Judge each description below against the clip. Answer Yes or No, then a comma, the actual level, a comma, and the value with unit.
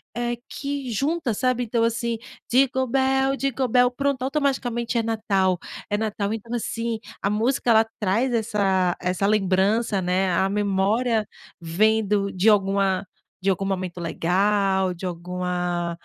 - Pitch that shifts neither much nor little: Yes, average, 4.0 semitones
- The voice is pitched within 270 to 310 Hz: No, high, 210 Hz